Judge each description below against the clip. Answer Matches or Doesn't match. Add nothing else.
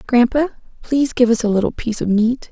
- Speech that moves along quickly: Matches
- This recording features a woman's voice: Matches